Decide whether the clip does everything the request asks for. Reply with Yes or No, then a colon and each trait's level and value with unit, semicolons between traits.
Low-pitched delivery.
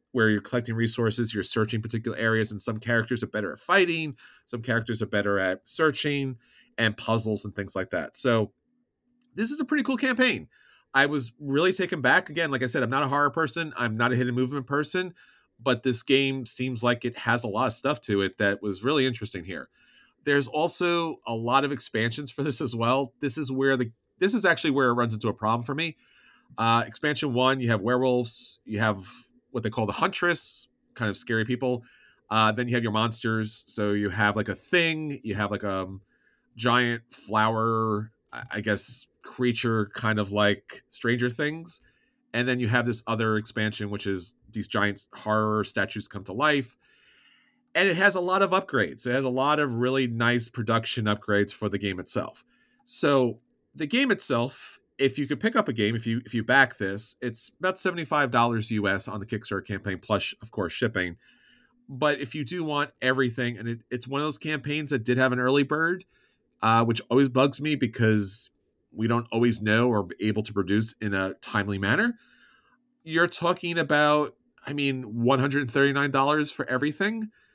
Yes: low, 125 Hz